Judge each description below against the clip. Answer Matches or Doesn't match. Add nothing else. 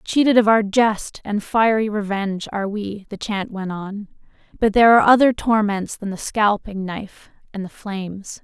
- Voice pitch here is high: Matches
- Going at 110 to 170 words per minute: Doesn't match